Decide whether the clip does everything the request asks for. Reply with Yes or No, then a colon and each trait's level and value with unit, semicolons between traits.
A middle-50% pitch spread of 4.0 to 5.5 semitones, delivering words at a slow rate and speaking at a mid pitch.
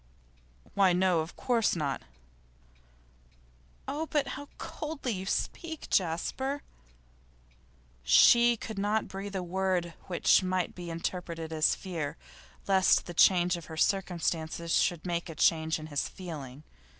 No: average, 3.2 semitones; slow, 130 wpm; medium, 180 Hz